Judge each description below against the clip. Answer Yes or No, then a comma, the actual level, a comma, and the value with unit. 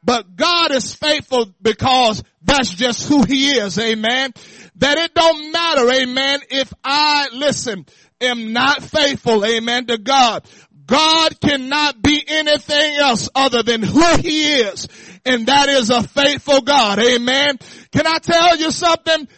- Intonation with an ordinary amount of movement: Yes, average, 3.7 semitones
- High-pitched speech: Yes, very high, 270 Hz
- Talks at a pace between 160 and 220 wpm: No, average, 145 wpm